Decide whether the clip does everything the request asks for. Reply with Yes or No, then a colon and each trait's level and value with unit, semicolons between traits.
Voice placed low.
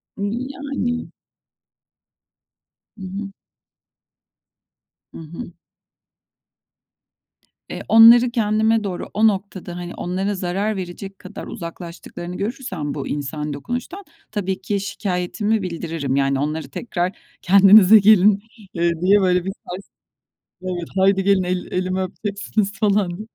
No: high, 195 Hz